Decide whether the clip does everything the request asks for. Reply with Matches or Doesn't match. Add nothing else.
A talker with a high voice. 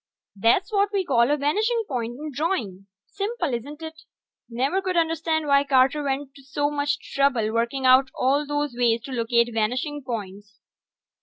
Matches